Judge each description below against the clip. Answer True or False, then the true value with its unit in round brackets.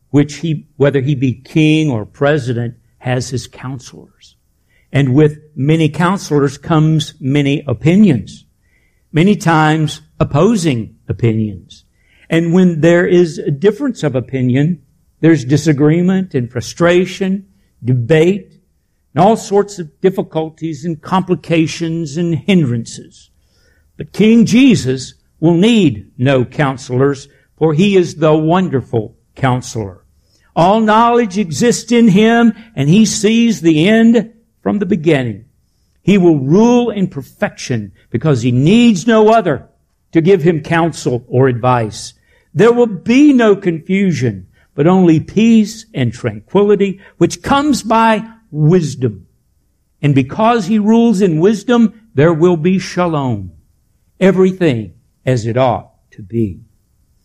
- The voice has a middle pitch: True (160 Hz)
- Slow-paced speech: True (120 wpm)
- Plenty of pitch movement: True (7.1 semitones)